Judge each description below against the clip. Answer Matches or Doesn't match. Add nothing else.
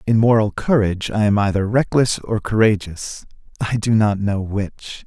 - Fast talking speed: Doesn't match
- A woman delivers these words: Doesn't match